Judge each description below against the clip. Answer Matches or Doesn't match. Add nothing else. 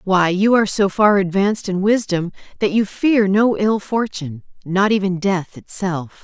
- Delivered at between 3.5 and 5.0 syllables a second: Matches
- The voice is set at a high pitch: Matches